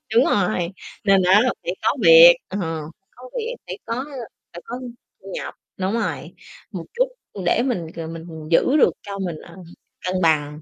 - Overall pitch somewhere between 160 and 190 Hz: Yes, medium, 185 Hz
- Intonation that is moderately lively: No, wide, 5.8 semitones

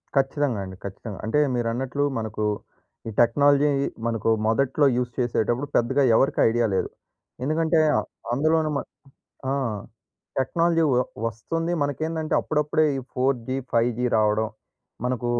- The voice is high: No, low, 130 Hz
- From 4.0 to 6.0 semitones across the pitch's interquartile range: Yes, average, 4.3 semitones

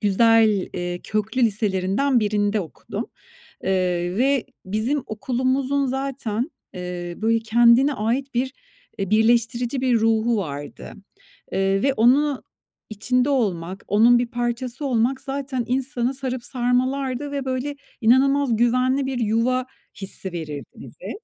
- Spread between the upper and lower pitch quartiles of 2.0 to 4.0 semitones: Yes, average, 3.6 semitones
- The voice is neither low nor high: No, high, 240 Hz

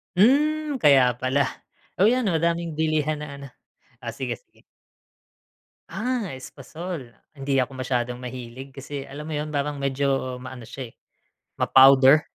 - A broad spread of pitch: No, average, 3.8 semitones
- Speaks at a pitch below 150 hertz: Yes, medium, 140 Hz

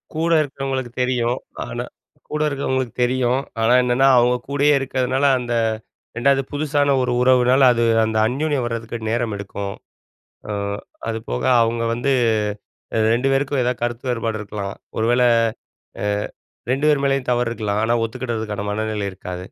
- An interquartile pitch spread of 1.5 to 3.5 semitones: Yes, average, 3.1 semitones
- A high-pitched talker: No, low, 125 Hz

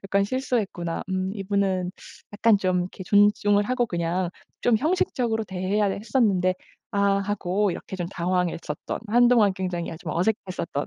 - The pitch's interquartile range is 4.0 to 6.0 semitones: No, narrow, 2.6 semitones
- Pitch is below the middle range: No, high, 195 Hz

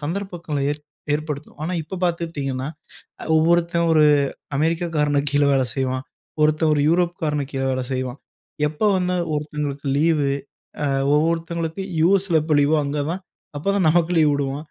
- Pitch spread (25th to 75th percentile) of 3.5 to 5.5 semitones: No, average, 2.8 semitones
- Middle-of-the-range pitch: Yes, medium, 155 Hz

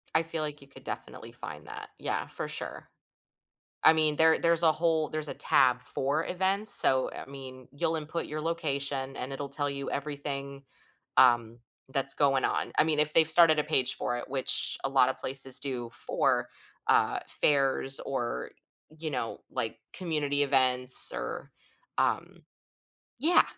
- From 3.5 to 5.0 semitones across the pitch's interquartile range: No, average, 2.9 semitones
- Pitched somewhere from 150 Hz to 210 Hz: No, medium, 140 Hz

